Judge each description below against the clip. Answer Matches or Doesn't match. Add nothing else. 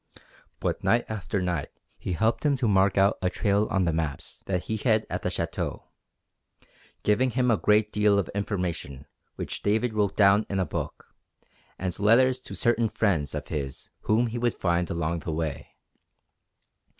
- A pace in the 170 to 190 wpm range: Matches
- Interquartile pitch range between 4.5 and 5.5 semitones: Doesn't match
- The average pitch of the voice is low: Matches